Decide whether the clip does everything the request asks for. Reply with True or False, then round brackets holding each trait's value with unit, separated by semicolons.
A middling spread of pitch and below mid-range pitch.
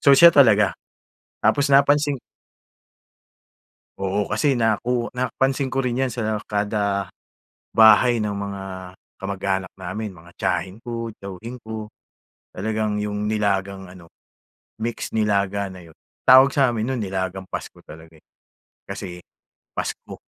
True (3.8 semitones; 105 Hz)